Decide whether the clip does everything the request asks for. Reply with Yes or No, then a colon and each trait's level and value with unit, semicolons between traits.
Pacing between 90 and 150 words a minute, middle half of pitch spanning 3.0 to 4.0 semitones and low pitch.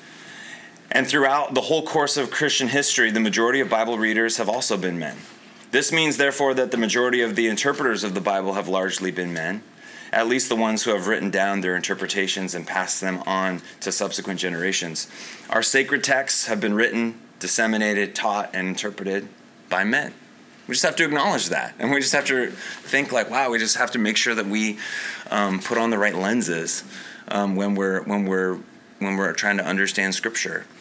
No: average, 195 wpm; average, 3.4 semitones; low, 105 Hz